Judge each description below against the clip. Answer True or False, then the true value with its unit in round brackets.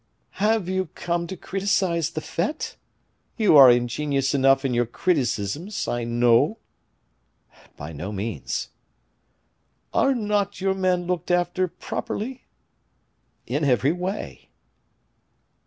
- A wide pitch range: True (7.1 semitones)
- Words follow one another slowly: True (110 wpm)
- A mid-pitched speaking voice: True (170 Hz)